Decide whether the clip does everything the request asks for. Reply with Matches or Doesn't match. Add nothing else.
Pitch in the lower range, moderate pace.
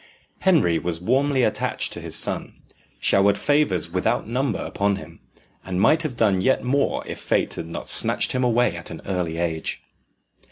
Matches